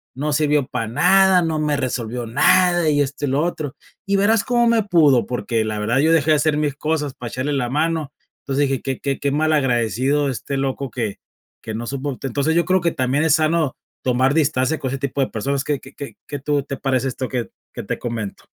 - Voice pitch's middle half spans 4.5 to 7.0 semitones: No, average, 3.3 semitones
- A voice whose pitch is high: No, medium, 140 Hz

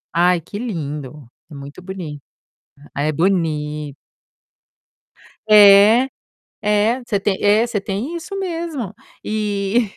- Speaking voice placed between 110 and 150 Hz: No, high, 200 Hz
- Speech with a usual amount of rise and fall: No, wide, 5.9 semitones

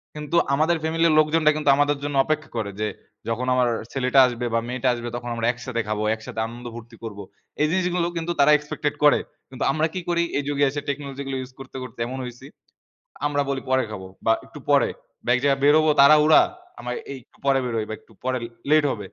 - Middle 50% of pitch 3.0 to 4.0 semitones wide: Yes, average, 3.7 semitones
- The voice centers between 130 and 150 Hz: Yes, low, 135 Hz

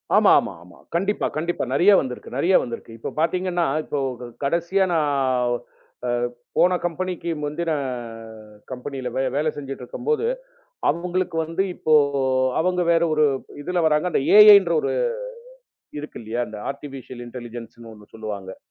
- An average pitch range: No, wide, 5.8 semitones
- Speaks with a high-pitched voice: No, medium, 150 Hz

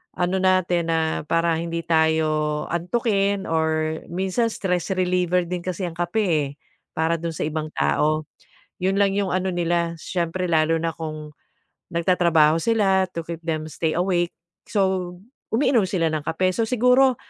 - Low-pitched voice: No, medium, 175 Hz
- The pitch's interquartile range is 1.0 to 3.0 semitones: Yes, average, 2.7 semitones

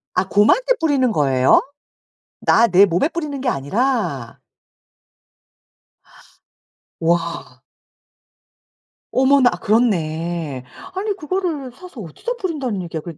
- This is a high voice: Yes, high, 220 Hz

